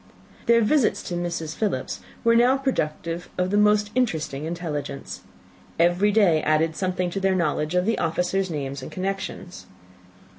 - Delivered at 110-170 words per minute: Yes, average, 150 wpm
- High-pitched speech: No, medium, 180 Hz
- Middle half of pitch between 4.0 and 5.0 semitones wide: Yes, average, 4.4 semitones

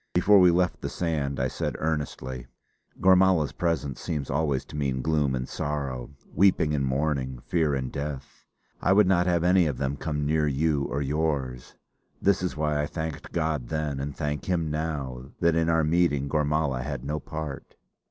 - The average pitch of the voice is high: No, very low, 75 Hz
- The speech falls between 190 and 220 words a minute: No, average, 180 wpm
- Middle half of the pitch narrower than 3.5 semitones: Yes, average, 3.0 semitones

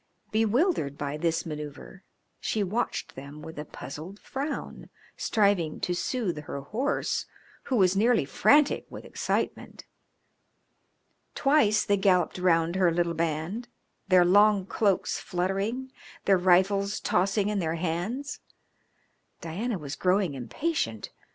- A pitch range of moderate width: Yes, average, 4.7 semitones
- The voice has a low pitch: No, medium, 185 Hz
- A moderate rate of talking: No, slow, 120 wpm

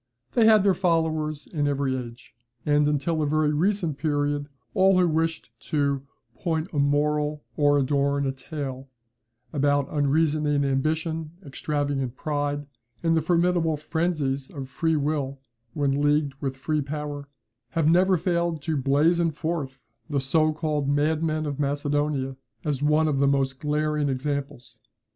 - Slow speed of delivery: No, average, 145 wpm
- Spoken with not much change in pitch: Yes, narrow, 2.0 semitones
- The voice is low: No, medium, 150 Hz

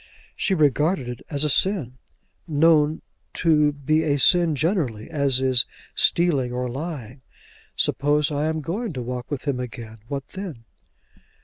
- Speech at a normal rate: Yes, average, 145 wpm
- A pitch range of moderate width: Yes, average, 4.0 semitones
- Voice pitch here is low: No, medium, 145 Hz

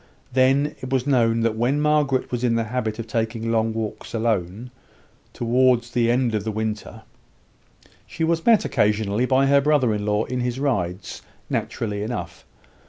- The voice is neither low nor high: No, low, 120 Hz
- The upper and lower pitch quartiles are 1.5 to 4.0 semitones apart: Yes, average, 2.9 semitones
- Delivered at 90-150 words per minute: No, average, 170 wpm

